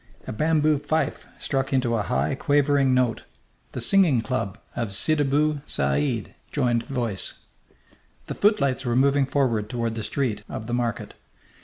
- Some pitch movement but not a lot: Yes, average, 3.8 semitones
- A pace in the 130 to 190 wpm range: Yes, average, 150 wpm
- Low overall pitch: Yes, low, 130 Hz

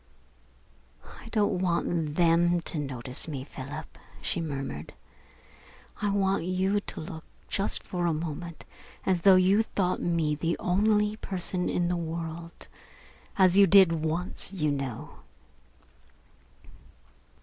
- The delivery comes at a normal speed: No, slow, 125 wpm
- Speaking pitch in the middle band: Yes, medium, 175 Hz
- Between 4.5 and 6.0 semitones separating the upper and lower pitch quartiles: No, average, 3.2 semitones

